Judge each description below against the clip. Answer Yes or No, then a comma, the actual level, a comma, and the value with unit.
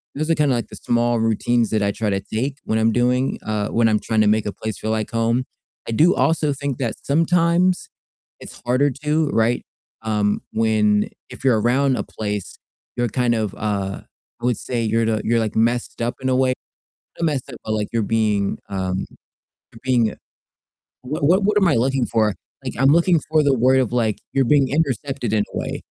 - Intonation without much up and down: No, average, 3.7 semitones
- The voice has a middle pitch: No, low, 120 Hz